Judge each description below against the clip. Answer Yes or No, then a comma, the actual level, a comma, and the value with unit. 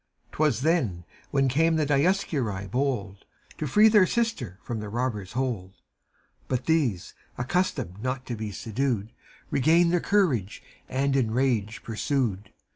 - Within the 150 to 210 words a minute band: No, average, 140 wpm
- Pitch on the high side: No, low, 130 Hz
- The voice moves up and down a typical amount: No, wide, 6.4 semitones